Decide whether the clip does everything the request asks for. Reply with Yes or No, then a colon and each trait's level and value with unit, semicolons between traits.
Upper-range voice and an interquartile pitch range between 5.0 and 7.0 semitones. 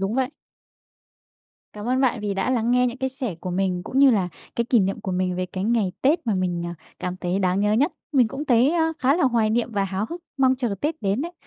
Yes: high, 225 Hz; average, 5.3 semitones